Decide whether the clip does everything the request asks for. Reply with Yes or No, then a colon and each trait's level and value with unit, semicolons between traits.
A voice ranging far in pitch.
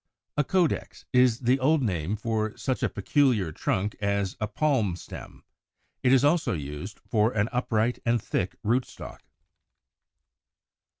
No: average, 4.4 semitones